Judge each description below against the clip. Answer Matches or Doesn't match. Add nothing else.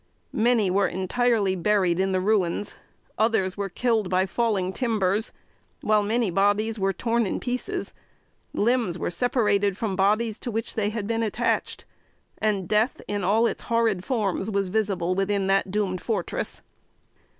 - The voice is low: Doesn't match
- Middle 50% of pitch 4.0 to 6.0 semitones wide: Doesn't match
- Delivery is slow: Doesn't match